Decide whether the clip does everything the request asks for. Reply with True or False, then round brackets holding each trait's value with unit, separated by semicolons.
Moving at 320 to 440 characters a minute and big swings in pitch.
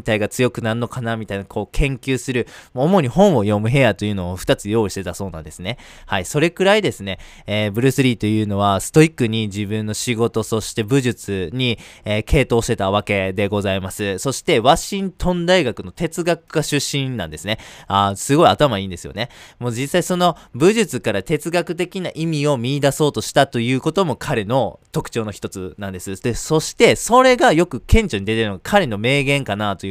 True (400 characters per minute; 6.4 semitones)